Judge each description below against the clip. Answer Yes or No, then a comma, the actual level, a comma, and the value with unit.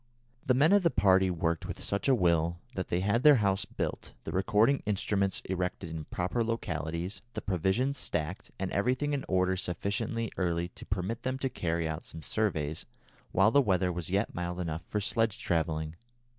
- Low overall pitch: Yes, very low, 95 Hz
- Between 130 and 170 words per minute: No, average, 185 wpm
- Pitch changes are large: No, average, 4.7 semitones